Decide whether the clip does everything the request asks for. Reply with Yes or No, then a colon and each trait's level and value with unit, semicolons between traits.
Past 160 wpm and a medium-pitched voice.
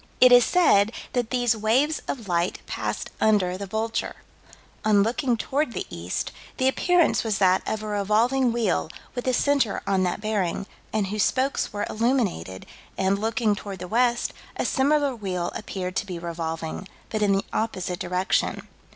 No: average, 170 wpm; high, 215 Hz